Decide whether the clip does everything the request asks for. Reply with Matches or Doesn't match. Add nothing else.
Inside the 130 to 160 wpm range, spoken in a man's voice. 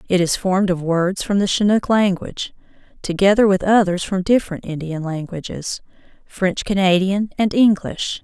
Doesn't match